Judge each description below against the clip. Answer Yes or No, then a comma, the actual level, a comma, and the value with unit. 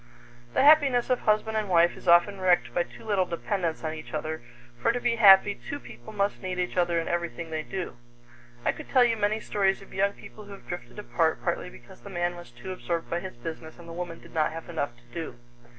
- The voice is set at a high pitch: No, medium, 180 Hz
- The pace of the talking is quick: Yes, fast, 235 wpm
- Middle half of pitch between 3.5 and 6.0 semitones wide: Yes, average, 3.8 semitones